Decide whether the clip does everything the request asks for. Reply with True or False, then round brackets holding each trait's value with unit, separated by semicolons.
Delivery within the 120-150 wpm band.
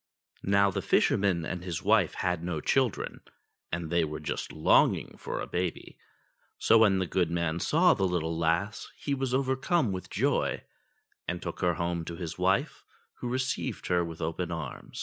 False (175 wpm)